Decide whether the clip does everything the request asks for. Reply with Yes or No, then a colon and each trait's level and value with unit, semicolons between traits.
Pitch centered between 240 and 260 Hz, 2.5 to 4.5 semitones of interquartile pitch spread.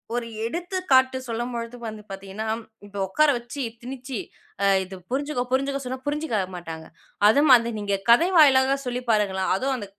Yes: high, 245 Hz; average, 4.2 semitones